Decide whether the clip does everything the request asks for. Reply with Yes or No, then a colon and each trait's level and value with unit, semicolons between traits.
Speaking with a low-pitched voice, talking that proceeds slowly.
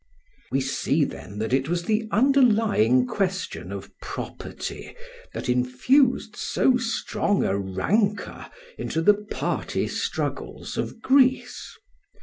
No: high, 195 Hz; slow, 120 wpm